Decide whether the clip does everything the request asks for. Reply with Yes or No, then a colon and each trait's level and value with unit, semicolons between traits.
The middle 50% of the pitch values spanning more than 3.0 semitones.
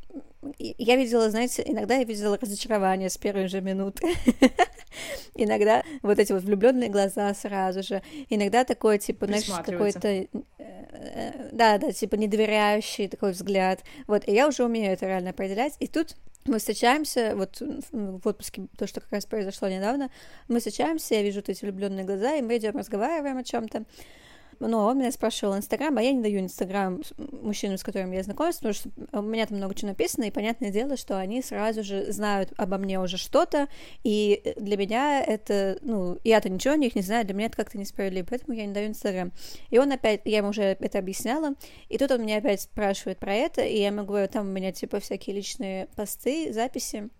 Yes: average, 3.6 semitones